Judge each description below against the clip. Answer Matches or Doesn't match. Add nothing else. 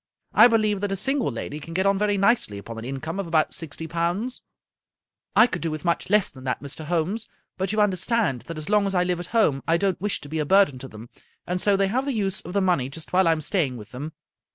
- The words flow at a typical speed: Doesn't match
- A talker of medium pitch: Matches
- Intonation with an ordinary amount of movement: Matches